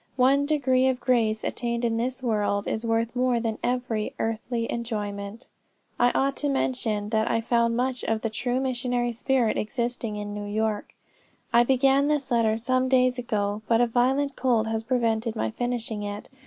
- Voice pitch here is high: Yes, high, 235 Hz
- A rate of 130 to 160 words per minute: No, average, 180 wpm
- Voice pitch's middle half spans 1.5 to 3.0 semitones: Yes, narrow, 2.5 semitones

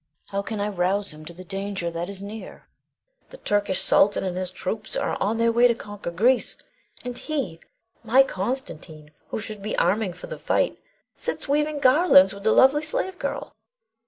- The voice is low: No, high, 205 Hz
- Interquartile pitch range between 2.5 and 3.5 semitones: No, average, 4.8 semitones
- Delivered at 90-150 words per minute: No, average, 185 wpm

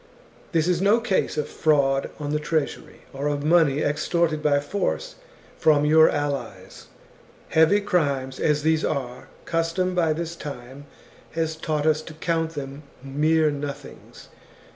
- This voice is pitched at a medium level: Yes, medium, 155 Hz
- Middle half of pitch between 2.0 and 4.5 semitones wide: Yes, narrow, 2.4 semitones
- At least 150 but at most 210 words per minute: No, average, 140 wpm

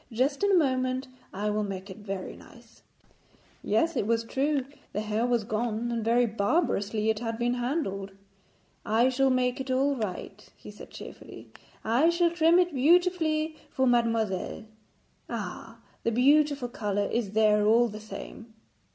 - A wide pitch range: No, average, 4.4 semitones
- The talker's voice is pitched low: No, high, 240 Hz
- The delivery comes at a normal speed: Yes, average, 160 wpm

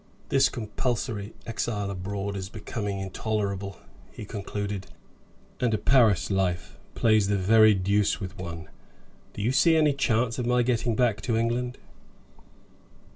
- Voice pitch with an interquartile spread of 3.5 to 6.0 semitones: No, average, 3.1 semitones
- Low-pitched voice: Yes, low, 105 Hz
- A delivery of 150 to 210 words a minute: No, slow, 135 wpm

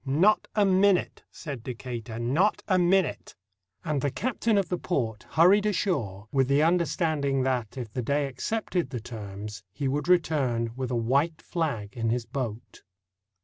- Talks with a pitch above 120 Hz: Yes, medium, 140 Hz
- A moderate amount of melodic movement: No, wide, 6.8 semitones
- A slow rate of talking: No, average, 160 wpm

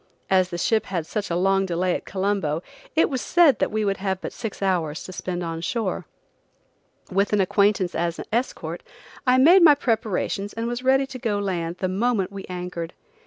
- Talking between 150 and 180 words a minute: No, average, 200 wpm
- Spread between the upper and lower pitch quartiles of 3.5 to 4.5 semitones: Yes, average, 4.2 semitones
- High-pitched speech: Yes, high, 195 Hz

